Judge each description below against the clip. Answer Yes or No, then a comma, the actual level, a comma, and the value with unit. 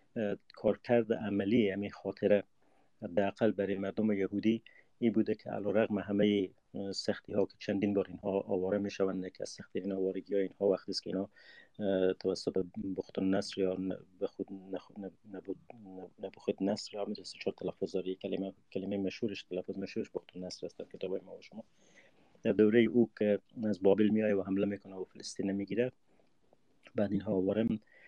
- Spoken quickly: Yes, fast, 160 wpm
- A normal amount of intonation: No, narrow, 1.7 semitones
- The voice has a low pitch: Yes, low, 100 Hz